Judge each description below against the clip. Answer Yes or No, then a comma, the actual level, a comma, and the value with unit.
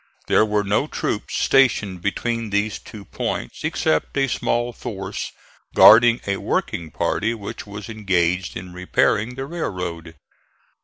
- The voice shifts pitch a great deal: No, average, 4.1 semitones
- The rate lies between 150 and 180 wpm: No, slow, 135 wpm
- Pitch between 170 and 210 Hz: No, low, 105 Hz